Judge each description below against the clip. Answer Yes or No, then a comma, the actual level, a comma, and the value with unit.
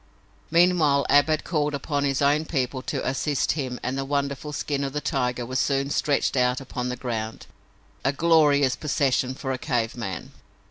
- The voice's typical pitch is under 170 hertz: Yes, medium, 140 Hz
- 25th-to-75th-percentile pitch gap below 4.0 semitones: Yes, narrow, 2.4 semitones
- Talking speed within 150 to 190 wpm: Yes, average, 180 wpm